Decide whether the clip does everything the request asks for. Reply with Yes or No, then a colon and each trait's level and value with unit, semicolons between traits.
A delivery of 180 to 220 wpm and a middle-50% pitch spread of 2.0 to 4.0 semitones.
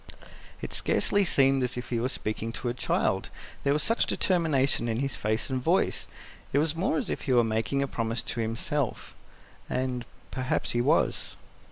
Yes: average, 185 wpm; average, 3.3 semitones